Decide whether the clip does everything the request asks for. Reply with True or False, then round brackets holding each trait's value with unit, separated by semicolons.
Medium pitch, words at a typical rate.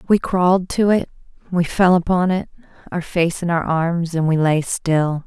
True (175 Hz; 195 wpm)